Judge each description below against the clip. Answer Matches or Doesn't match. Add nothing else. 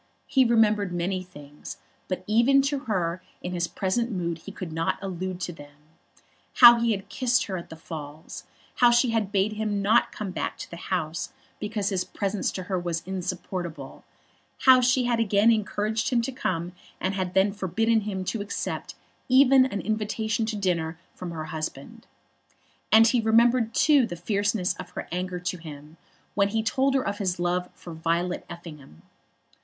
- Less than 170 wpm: Doesn't match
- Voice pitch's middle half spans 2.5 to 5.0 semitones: Matches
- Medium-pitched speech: Doesn't match